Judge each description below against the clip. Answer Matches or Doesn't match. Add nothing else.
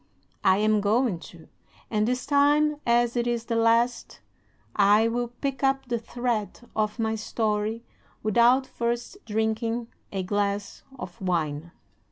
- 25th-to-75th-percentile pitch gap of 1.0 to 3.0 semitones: Matches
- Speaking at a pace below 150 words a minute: Matches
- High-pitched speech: Matches